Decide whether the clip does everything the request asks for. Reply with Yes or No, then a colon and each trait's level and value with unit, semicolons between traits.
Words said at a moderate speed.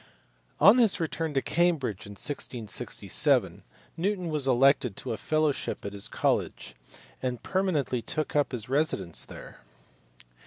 No: slow, 130 wpm